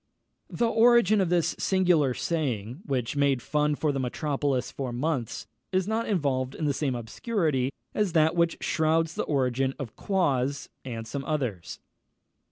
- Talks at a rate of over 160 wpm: No, average, 155 wpm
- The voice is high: No, medium, 145 Hz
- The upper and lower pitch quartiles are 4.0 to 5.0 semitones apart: Yes, average, 4.7 semitones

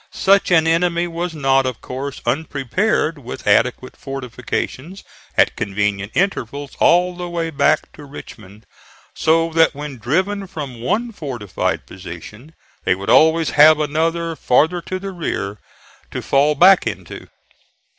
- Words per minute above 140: No, slow, 135 wpm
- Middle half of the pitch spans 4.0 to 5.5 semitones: Yes, average, 5.1 semitones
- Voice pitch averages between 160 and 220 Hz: No, medium, 150 Hz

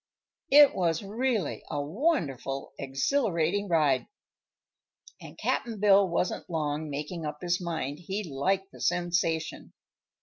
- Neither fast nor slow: No, slow, 115 wpm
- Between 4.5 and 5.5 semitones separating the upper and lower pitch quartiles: Yes, average, 5.0 semitones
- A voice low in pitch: No, medium, 170 Hz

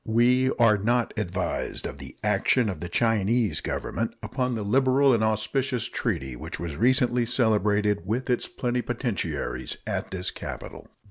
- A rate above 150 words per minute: No, average, 145 wpm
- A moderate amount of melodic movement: Yes, average, 4.0 semitones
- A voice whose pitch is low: Yes, low, 110 Hz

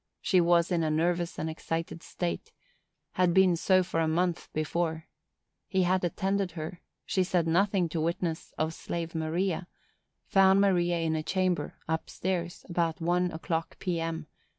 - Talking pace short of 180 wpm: Yes, average, 160 wpm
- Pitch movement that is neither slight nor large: No, narrow, 2.1 semitones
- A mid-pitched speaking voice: Yes, medium, 170 Hz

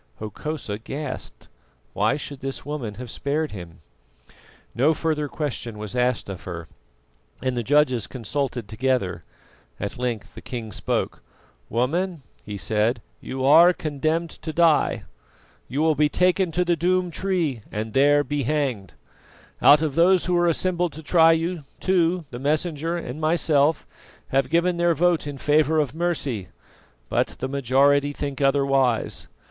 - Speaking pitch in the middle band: Yes, medium, 145 Hz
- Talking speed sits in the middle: Yes, average, 150 wpm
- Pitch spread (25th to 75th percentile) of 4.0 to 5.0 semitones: Yes, average, 4.7 semitones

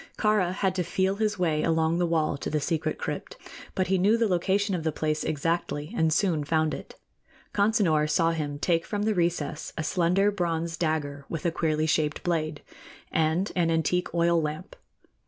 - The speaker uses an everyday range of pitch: Yes, average, 3.0 semitones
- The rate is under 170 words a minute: No, average, 185 wpm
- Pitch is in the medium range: Yes, medium, 165 Hz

